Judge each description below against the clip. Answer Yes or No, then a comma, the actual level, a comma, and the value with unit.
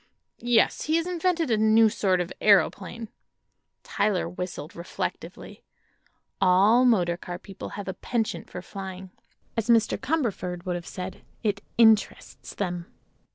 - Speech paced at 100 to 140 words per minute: Yes, slow, 135 wpm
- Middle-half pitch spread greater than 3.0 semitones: Yes, average, 4.2 semitones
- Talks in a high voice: Yes, high, 200 Hz